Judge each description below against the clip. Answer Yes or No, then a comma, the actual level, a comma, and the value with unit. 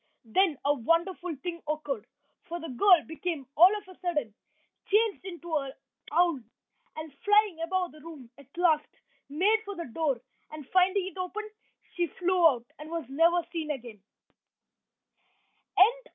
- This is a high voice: Yes, very high, 335 Hz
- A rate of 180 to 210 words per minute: No, average, 150 wpm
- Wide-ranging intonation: No, average, 3.6 semitones